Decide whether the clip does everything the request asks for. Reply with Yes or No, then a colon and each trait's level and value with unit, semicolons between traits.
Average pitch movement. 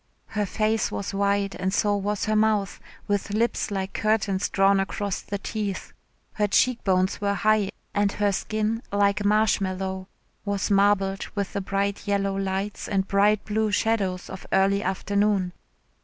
No: narrow, 1.3 semitones